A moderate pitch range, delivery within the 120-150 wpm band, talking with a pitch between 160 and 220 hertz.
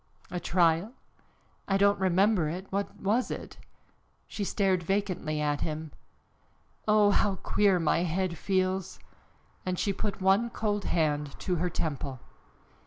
Yes: average, 3.4 semitones; slow, 135 wpm; medium, 185 Hz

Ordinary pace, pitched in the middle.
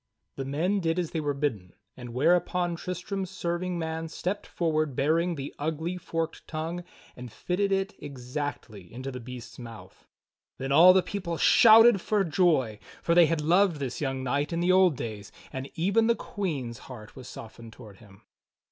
Yes: average, 175 wpm; medium, 160 Hz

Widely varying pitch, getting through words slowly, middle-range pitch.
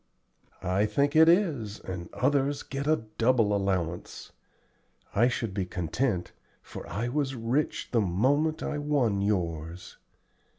No: wide, 6.8 semitones; slow, 130 wpm; low, 115 Hz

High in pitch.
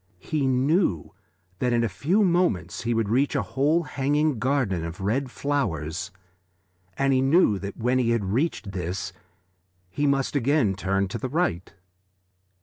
No: low, 125 Hz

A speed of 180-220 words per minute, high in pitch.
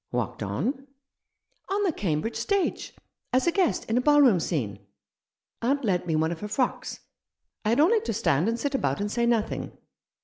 Yes: average, 190 wpm; high, 230 Hz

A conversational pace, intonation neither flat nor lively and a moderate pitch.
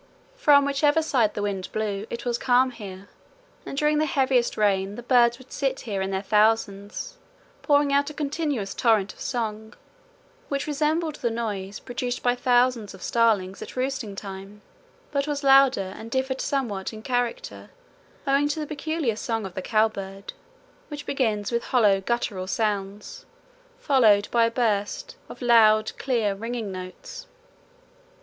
No: average, 155 wpm; average, 5.0 semitones; high, 235 Hz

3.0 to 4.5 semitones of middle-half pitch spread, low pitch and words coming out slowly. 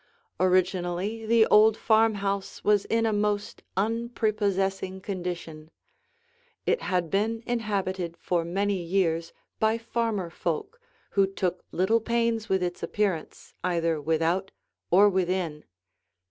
No: average, 3.5 semitones; high, 195 Hz; slow, 115 wpm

